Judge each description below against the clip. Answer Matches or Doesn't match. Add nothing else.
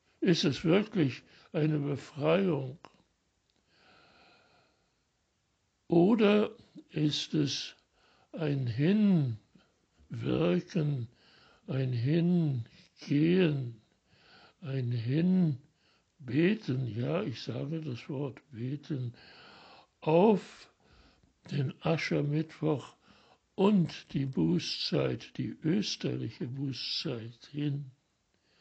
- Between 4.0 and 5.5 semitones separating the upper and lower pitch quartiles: Matches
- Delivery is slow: Matches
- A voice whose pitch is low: Doesn't match